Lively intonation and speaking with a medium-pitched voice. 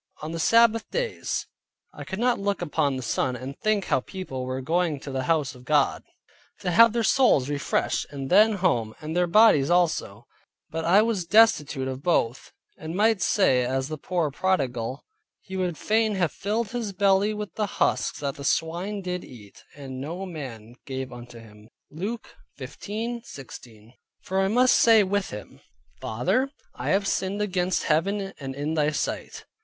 Yes: wide, 7.2 semitones; medium, 170 Hz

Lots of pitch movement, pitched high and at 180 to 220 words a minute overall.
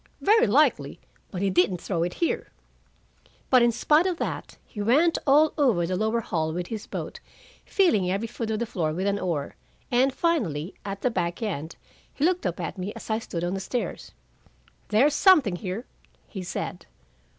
Yes: wide, 6.5 semitones; high, 210 Hz; average, 185 wpm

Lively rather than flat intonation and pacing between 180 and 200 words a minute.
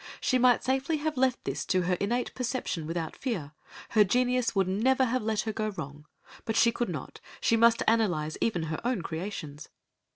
Yes: wide, 6.1 semitones; average, 190 wpm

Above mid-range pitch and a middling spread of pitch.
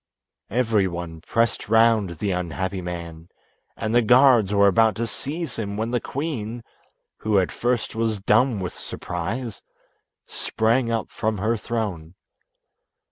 No: low, 110 Hz; average, 3.6 semitones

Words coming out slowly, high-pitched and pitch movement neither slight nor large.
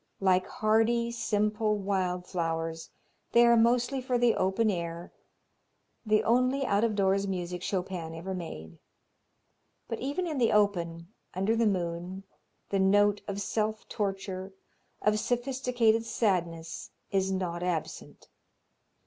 Yes: slow, 125 wpm; high, 200 Hz; average, 4.0 semitones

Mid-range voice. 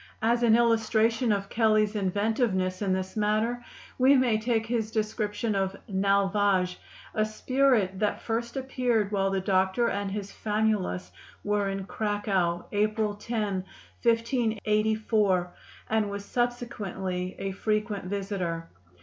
No: high, 210 Hz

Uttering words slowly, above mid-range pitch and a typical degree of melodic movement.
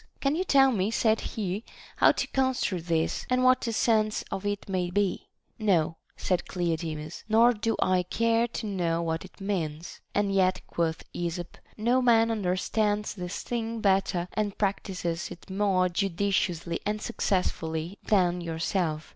No: average, 155 wpm; high, 195 Hz; average, 3.9 semitones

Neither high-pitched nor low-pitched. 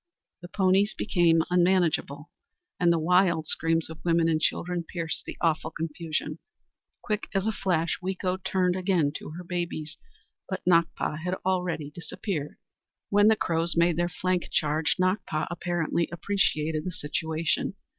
Yes: medium, 170 Hz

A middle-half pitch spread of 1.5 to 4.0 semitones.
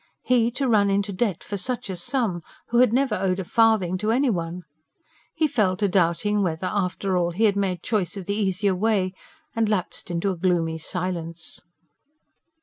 Yes: average, 3.3 semitones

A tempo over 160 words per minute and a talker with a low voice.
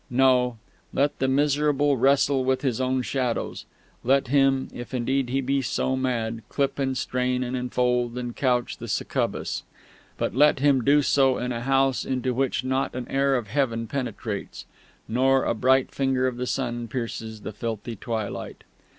Yes: average, 170 wpm; low, 130 Hz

